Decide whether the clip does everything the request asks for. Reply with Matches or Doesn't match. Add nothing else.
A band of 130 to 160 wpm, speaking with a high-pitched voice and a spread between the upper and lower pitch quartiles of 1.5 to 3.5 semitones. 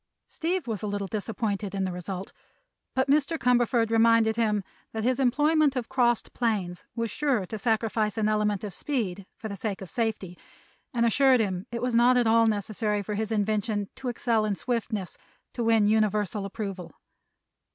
Doesn't match